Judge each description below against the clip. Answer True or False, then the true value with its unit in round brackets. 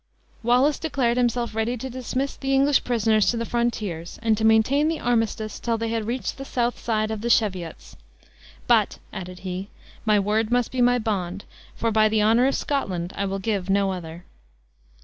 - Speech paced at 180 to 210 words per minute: True (190 wpm)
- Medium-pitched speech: False (225 Hz)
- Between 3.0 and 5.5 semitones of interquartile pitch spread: True (3.3 semitones)